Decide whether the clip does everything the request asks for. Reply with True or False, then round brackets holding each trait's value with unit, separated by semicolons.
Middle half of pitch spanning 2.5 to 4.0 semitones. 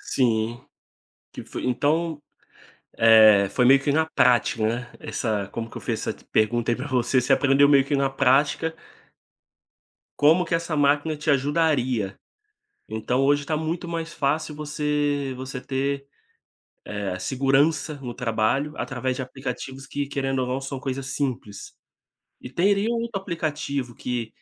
True (3.2 semitones)